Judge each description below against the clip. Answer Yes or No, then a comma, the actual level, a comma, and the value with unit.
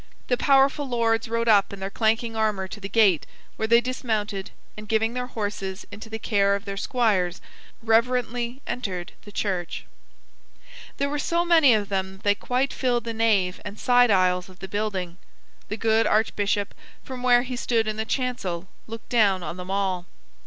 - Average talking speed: Yes, average, 180 wpm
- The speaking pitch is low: No, high, 220 Hz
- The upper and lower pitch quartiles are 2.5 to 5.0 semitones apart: Yes, average, 3.6 semitones